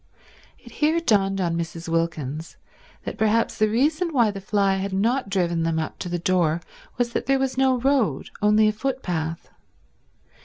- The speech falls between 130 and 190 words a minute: Yes, average, 170 wpm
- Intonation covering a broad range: Yes, wide, 6.8 semitones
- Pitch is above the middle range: Yes, high, 200 Hz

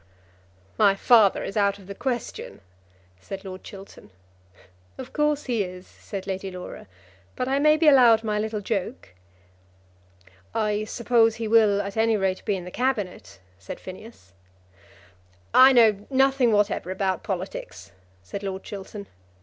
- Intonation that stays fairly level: No, average, 3.4 semitones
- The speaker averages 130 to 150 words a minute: Yes, average, 145 wpm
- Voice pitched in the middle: No, high, 205 Hz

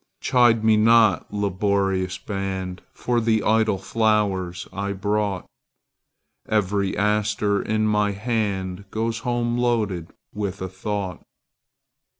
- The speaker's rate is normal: No, slow, 95 wpm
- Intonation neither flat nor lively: No, narrow, 2.3 semitones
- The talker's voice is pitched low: Yes, low, 105 Hz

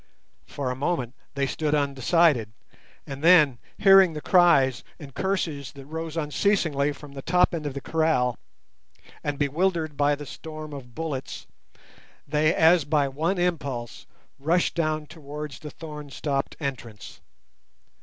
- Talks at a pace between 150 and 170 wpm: No, average, 140 wpm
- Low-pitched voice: No, medium, 150 Hz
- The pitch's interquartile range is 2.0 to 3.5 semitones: Yes, average, 2.9 semitones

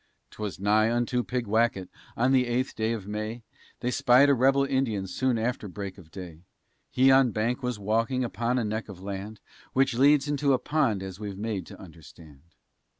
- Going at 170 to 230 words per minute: Yes, average, 190 wpm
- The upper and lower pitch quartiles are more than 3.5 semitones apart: Yes, average, 4.1 semitones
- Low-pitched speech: Yes, low, 115 Hz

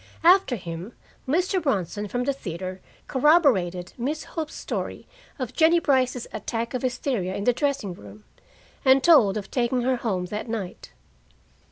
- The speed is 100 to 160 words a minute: Yes, average, 150 wpm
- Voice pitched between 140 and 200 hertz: No, high, 245 Hz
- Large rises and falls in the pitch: Yes, wide, 6.5 semitones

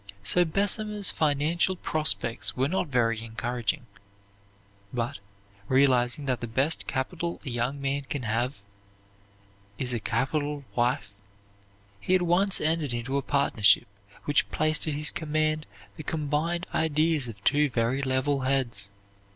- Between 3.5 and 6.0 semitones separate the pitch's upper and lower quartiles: Yes, average, 4.2 semitones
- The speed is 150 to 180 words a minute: No, slow, 135 wpm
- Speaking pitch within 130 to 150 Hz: Yes, medium, 140 Hz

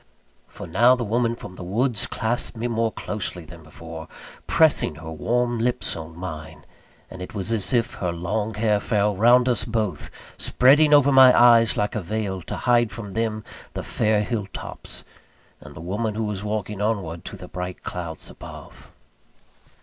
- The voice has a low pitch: Yes, low, 105 Hz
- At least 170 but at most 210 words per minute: Yes, average, 175 wpm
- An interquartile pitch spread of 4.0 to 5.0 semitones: Yes, average, 4.5 semitones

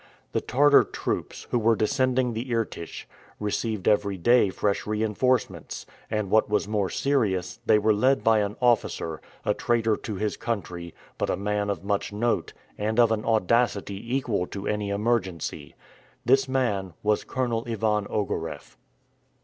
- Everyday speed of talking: Yes, average, 150 wpm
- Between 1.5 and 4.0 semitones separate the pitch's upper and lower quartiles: Yes, average, 2.8 semitones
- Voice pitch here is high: No, low, 105 Hz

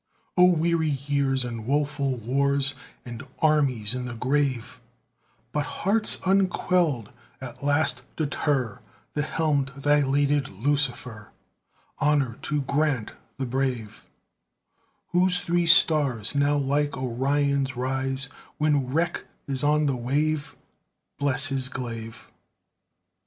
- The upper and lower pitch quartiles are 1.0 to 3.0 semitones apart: Yes, narrow, 2.6 semitones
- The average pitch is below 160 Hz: Yes, medium, 140 Hz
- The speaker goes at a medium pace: No, slow, 110 wpm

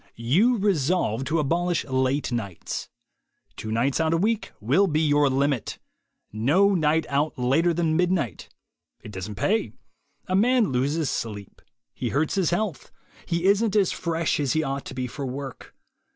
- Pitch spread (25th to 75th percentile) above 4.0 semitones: Yes, average, 5.3 semitones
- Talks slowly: No, average, 160 wpm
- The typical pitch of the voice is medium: Yes, medium, 155 Hz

